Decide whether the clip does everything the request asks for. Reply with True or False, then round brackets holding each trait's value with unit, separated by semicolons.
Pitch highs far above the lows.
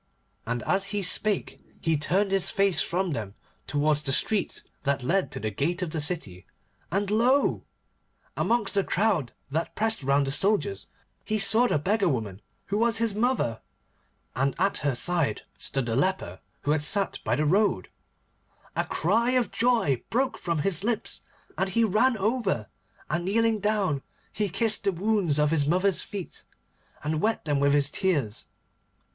True (6.6 semitones)